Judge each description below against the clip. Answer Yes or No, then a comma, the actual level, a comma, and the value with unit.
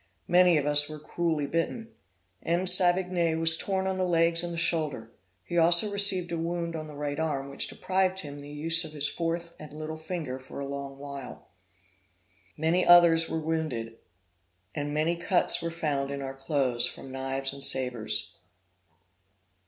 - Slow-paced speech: No, average, 175 wpm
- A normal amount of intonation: Yes, average, 3.5 semitones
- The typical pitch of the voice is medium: Yes, medium, 160 Hz